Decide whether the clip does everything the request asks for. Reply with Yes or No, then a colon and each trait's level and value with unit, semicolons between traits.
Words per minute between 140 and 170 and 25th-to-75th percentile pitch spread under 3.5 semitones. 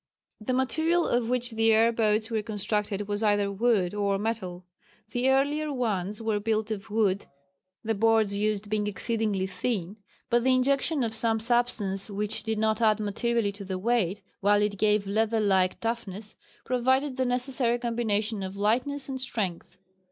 Yes: average, 165 wpm; average, 2.8 semitones